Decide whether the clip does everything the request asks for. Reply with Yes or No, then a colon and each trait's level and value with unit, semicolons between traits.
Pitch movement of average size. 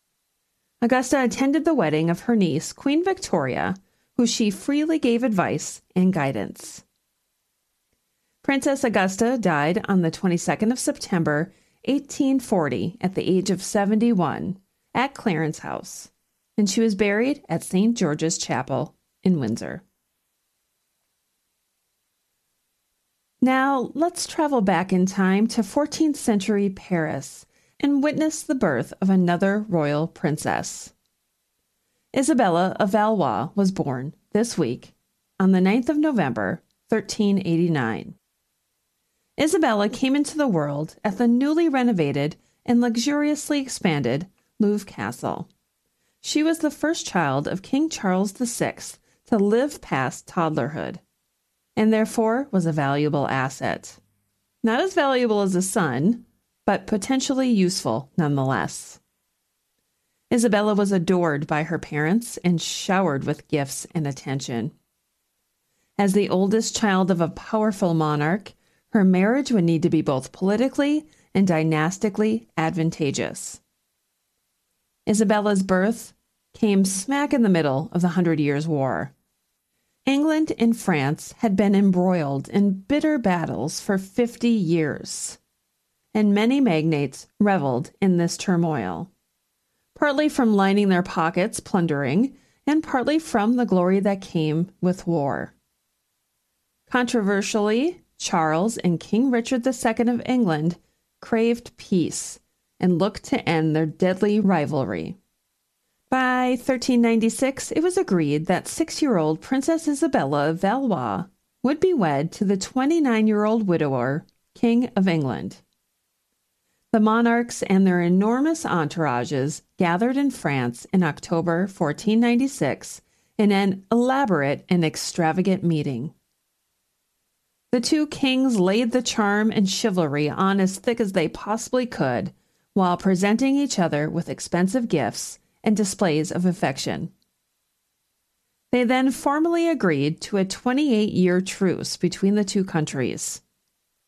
No: wide, 6.6 semitones